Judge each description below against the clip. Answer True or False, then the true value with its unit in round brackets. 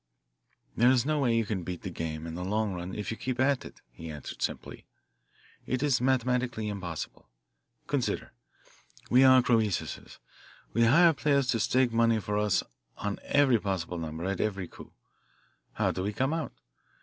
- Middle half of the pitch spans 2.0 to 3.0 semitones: False (5.5 semitones)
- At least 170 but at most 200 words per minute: True (175 wpm)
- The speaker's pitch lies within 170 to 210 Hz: False (110 Hz)